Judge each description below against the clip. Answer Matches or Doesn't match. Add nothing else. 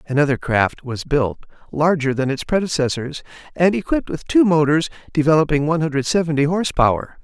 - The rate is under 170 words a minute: Matches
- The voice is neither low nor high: Matches